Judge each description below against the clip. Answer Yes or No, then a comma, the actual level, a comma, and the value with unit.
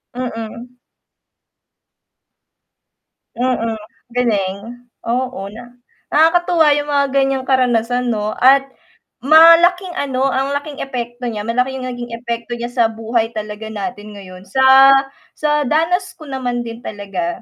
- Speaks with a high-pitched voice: Yes, high, 245 Hz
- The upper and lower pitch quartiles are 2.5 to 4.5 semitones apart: Yes, average, 3.1 semitones